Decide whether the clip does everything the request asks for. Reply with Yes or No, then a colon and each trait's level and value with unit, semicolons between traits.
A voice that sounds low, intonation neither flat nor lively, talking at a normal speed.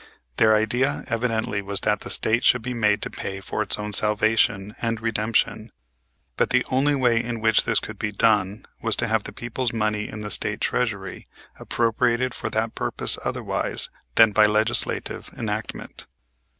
No: low, 110 Hz; narrow, 1.8 semitones; average, 170 wpm